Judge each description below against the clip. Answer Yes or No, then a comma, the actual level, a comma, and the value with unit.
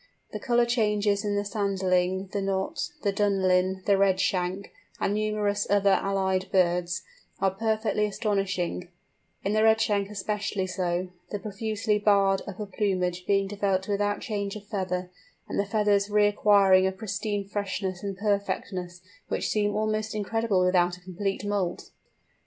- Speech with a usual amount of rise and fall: No, narrow, 1.7 semitones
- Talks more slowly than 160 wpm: Yes, average, 140 wpm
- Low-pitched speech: No, high, 200 Hz